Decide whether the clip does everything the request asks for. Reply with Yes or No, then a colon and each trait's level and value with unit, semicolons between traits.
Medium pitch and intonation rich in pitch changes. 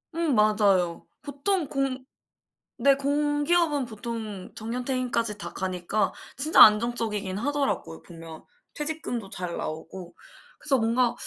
No: high, 235 Hz; wide, 5.7 semitones